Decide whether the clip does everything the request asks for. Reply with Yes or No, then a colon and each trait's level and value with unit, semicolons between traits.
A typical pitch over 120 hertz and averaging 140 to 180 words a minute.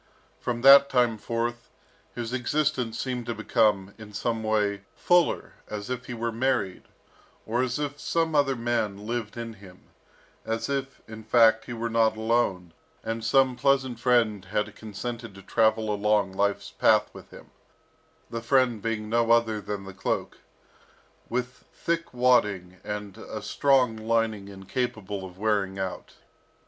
No: low, 115 Hz; average, 150 wpm